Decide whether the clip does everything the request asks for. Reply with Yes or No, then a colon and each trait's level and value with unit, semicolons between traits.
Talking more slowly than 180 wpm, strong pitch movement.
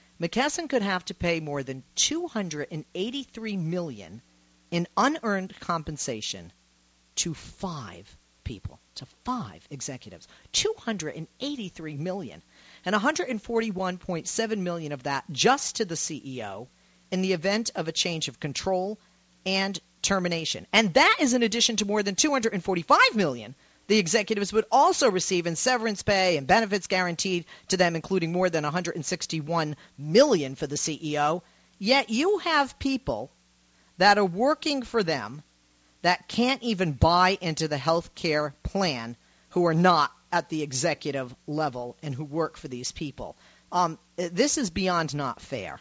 Yes: average, 140 wpm; wide, 6.0 semitones